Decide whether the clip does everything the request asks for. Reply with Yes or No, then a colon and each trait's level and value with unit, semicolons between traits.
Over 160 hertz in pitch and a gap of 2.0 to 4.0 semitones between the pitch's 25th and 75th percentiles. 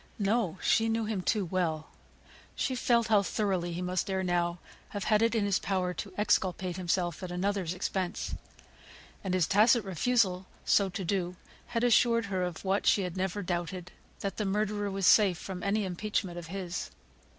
Yes: high, 190 Hz; narrow, 2.6 semitones